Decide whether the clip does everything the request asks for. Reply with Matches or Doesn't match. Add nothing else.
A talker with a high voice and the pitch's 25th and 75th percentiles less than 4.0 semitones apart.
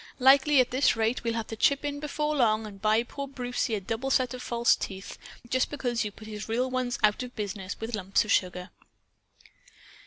Matches